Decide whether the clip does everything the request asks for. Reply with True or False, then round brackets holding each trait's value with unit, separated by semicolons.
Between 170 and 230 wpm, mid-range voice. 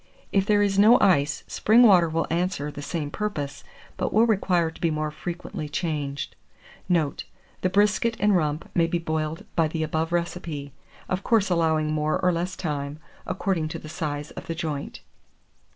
True (175 wpm; 165 Hz)